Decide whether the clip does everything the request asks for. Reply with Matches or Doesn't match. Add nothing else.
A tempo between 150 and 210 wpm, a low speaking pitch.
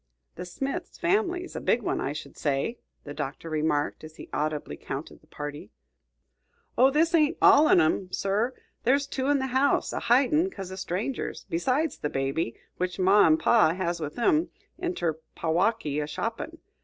Doesn't match